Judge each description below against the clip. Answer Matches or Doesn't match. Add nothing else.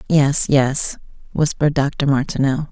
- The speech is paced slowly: Matches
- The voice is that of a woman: Matches